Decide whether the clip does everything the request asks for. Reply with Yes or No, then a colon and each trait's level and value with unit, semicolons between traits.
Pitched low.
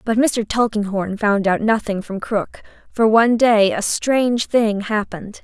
No: high, 215 Hz